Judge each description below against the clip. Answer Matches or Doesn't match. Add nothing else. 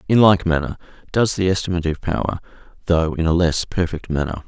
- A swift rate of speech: Doesn't match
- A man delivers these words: Matches